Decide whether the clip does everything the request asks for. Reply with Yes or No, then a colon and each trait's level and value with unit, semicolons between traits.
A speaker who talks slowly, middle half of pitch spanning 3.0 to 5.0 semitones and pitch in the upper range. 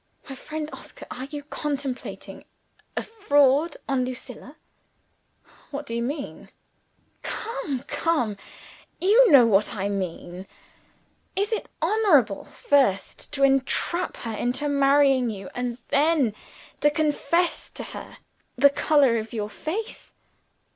Yes: slow, 120 wpm; average, 4.2 semitones; very high, 275 Hz